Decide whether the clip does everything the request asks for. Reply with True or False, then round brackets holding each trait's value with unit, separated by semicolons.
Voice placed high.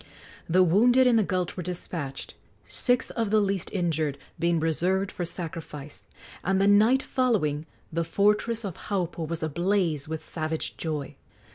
False (175 Hz)